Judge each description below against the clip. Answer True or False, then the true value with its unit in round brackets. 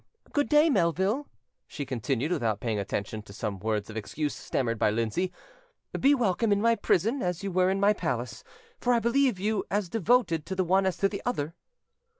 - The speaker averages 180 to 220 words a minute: True (195 wpm)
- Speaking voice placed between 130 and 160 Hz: False (180 Hz)